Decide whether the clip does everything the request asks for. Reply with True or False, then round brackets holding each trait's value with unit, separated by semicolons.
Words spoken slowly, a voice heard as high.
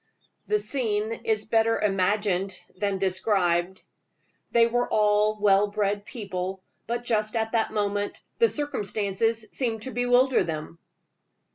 True (125 wpm; 210 Hz)